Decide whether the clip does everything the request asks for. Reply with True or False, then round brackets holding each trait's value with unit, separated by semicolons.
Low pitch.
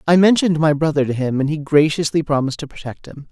False (150 Hz)